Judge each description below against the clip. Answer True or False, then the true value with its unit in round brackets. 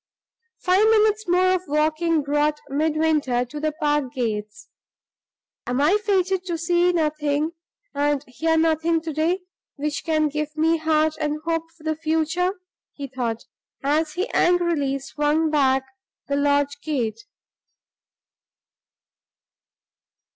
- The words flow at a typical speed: False (125 wpm)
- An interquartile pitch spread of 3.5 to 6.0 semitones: False (2.5 semitones)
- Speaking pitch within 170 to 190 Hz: False (310 Hz)